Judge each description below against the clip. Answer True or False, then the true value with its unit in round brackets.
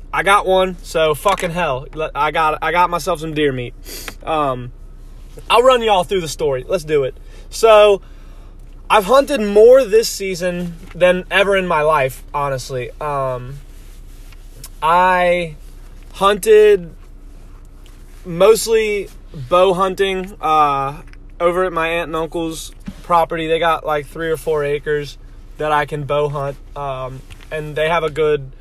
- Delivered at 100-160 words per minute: True (145 wpm)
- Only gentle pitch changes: False (4.5 semitones)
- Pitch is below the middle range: False (165 Hz)